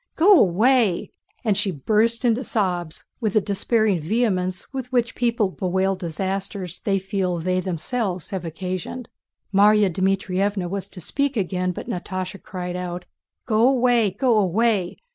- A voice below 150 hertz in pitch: No, high, 195 Hz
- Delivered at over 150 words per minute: No, average, 145 wpm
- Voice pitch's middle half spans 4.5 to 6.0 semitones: No, average, 3.8 semitones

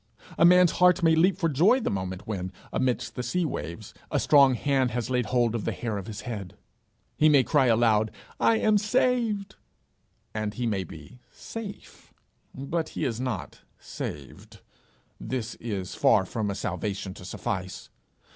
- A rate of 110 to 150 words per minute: No, average, 165 wpm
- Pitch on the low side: Yes, low, 125 Hz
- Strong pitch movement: Yes, wide, 8.0 semitones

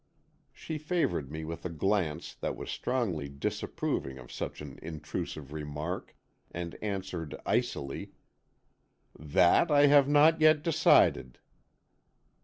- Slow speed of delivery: Yes, slow, 115 wpm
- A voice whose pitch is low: Yes, very low, 85 Hz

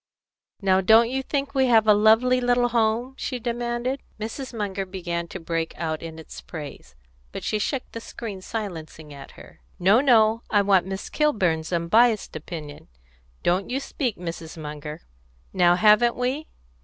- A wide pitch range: Yes, wide, 5.9 semitones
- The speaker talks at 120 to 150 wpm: No, average, 160 wpm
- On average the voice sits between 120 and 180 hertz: No, high, 210 Hz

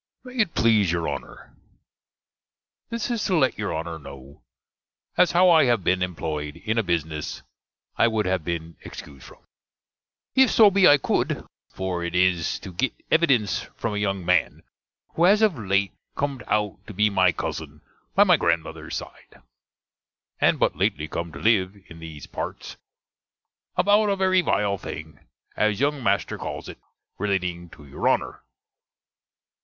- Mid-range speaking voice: No, low, 100 Hz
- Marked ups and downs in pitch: Yes, wide, 8.7 semitones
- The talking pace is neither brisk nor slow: Yes, average, 160 wpm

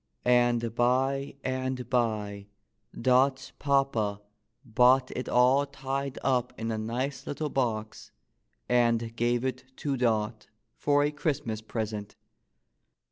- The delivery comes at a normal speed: No, slow, 120 wpm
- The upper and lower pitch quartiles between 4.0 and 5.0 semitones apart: No, average, 2.9 semitones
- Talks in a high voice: No, low, 125 Hz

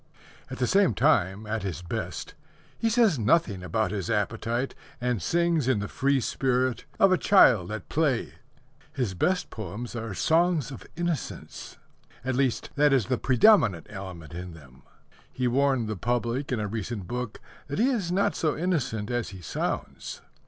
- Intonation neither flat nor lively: No, wide, 6.2 semitones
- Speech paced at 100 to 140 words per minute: No, average, 165 wpm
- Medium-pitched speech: No, low, 125 Hz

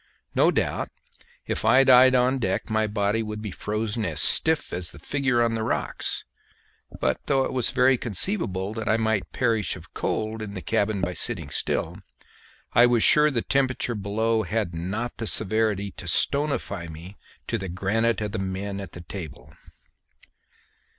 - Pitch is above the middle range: No, low, 110 Hz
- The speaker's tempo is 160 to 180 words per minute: Yes, average, 170 wpm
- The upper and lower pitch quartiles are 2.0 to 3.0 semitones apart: No, average, 3.7 semitones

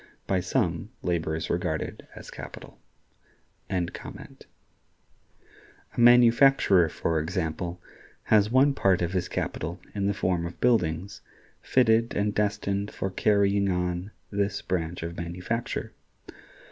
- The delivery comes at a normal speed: No, slow, 115 wpm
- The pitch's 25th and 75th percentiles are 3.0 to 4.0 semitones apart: Yes, average, 3.3 semitones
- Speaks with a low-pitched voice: Yes, very low, 95 Hz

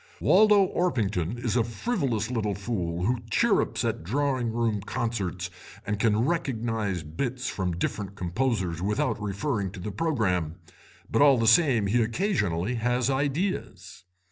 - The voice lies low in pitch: Yes, low, 115 Hz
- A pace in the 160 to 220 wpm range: No, average, 140 wpm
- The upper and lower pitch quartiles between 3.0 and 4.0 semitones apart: No, average, 5.0 semitones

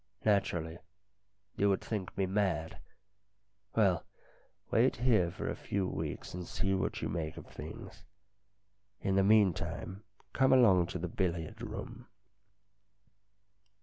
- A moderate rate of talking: No, slow, 130 wpm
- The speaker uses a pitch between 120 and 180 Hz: No, very low, 95 Hz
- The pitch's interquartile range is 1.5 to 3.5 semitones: Yes, average, 3.1 semitones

